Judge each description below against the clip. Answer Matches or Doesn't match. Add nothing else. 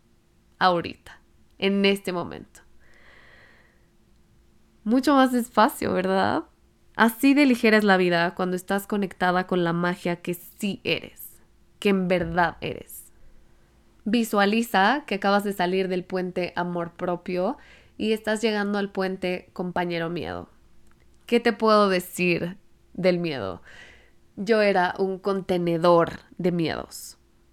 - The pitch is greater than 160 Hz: Matches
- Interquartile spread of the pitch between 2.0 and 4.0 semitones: Matches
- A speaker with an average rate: Doesn't match